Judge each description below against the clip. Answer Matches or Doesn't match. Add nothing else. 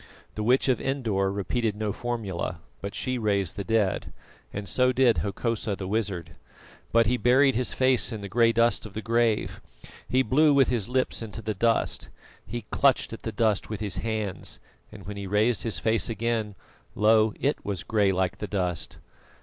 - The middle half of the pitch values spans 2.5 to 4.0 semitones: Matches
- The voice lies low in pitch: Matches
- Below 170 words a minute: Doesn't match